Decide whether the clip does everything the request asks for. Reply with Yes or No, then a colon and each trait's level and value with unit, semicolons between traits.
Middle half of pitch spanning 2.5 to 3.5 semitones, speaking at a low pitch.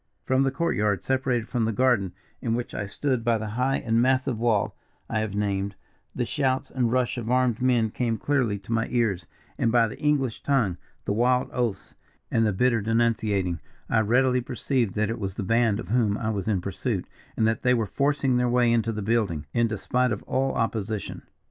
Yes: average, 3.0 semitones; low, 115 Hz